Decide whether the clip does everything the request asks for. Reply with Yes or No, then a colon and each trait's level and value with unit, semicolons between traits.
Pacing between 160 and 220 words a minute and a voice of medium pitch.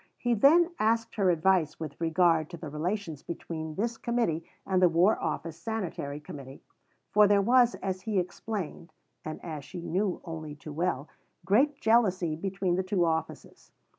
Yes: average, 165 wpm; medium, 180 Hz